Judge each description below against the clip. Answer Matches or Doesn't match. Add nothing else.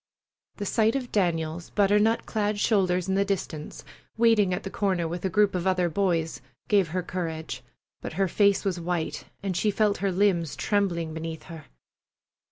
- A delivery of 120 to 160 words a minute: Doesn't match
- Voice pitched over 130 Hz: Matches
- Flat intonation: Doesn't match